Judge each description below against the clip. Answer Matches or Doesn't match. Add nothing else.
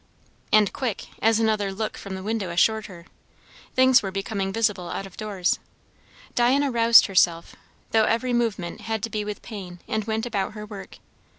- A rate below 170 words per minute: Doesn't match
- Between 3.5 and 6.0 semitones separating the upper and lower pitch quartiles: Doesn't match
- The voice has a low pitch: Doesn't match